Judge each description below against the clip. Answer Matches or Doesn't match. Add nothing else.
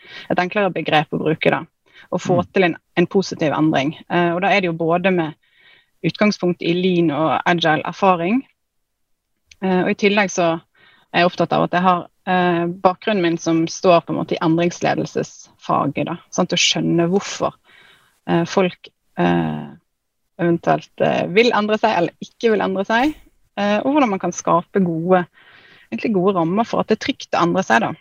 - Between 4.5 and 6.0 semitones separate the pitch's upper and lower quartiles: Doesn't match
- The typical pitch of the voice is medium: Matches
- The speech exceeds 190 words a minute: Doesn't match